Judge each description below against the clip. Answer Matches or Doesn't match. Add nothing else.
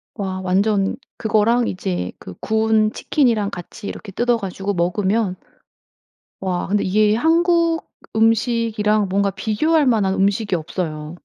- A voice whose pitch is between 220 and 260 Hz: Doesn't match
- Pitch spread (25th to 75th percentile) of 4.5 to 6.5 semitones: Doesn't match